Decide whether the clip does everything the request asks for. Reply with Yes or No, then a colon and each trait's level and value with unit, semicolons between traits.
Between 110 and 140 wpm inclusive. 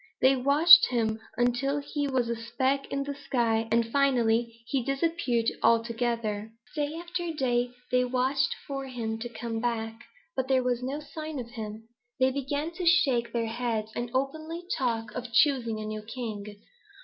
No: average, 165 wpm